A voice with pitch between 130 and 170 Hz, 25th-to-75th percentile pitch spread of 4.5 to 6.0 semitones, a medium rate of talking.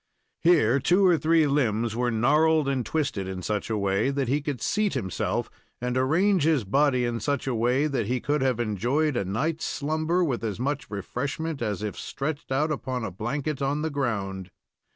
Yes: low, 135 Hz; average, 5.1 semitones; average, 195 wpm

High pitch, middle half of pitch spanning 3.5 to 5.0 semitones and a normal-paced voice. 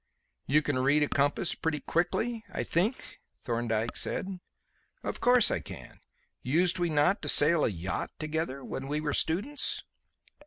No: medium, 155 Hz; average, 4.4 semitones; average, 155 wpm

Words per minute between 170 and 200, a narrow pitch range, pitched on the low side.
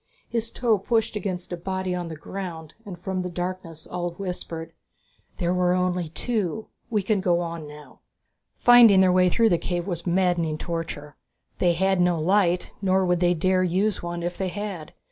No: average, 185 wpm; narrow, 2.0 semitones; medium, 180 Hz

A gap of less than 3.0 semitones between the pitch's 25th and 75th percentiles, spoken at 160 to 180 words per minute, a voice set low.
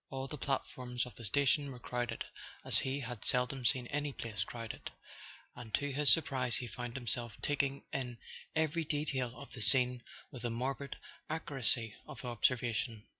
Yes: narrow, 2.6 semitones; average, 170 wpm; low, 125 Hz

